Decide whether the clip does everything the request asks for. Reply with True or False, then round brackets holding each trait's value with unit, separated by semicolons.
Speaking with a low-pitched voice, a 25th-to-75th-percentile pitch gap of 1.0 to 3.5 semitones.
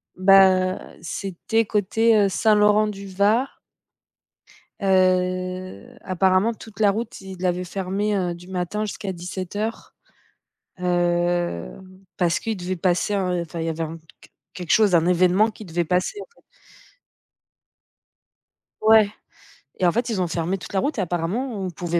False (185 Hz; 2.8 semitones)